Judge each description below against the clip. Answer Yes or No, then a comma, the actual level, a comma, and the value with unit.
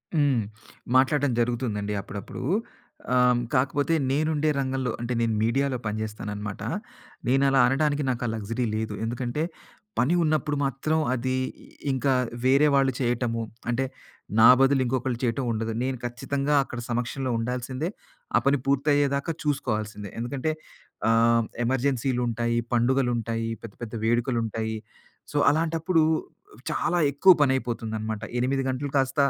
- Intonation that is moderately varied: Yes, average, 3.1 semitones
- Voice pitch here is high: No, low, 130 Hz